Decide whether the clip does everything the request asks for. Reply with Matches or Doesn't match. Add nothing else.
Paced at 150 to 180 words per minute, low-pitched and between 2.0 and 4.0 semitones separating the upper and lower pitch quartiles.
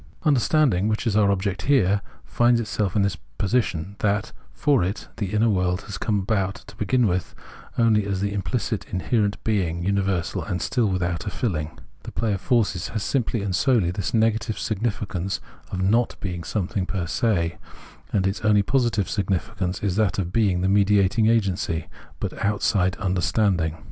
Matches